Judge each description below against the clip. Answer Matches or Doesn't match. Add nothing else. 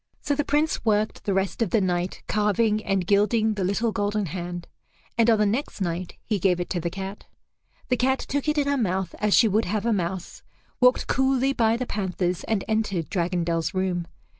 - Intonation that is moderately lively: Matches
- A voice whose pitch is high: Matches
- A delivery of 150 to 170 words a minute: Doesn't match